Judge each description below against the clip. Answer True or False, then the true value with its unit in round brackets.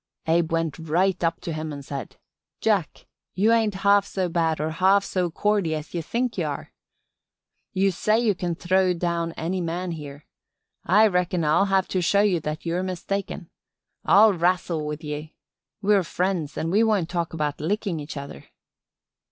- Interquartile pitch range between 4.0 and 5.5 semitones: False (3.4 semitones)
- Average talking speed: True (175 wpm)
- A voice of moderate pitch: True (175 Hz)